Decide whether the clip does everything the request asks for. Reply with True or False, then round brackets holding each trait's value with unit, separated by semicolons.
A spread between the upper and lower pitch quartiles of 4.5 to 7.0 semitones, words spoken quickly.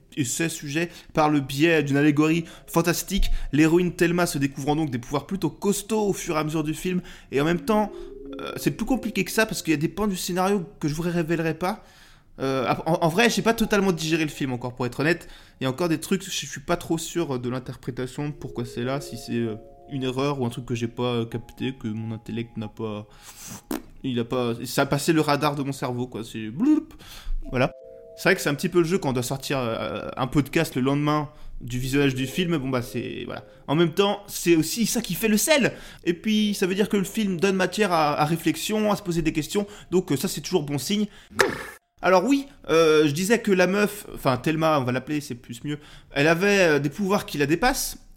True (5.4 semitones; 245 wpm)